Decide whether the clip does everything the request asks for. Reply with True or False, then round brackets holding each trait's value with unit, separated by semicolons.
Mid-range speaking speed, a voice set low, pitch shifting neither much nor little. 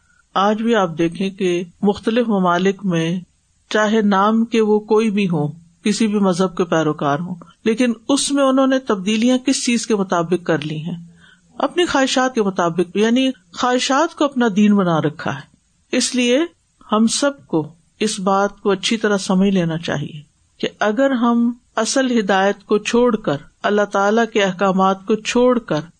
False (170 wpm; 210 Hz; 4.8 semitones)